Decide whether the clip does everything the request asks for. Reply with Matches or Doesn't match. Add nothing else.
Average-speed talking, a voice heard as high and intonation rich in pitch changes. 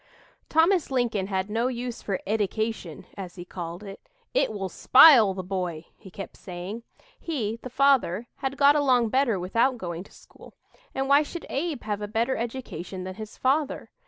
Matches